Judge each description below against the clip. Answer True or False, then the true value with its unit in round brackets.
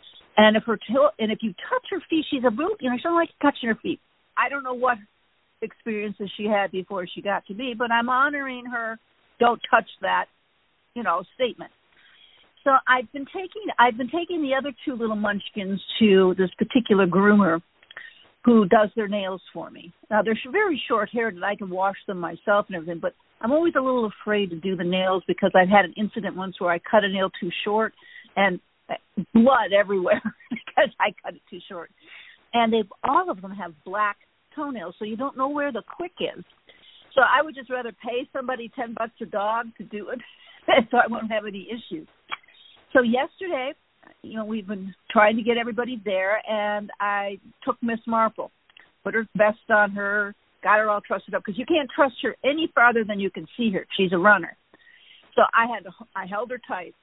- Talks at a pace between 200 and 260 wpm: True (205 wpm)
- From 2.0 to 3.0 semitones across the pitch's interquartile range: False (4.2 semitones)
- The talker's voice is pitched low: False (225 Hz)